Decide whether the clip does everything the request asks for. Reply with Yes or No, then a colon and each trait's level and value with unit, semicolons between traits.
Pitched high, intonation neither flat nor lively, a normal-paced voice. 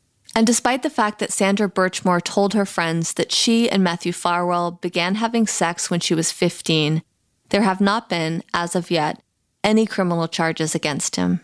No: medium, 180 Hz; average, 3.6 semitones; average, 180 wpm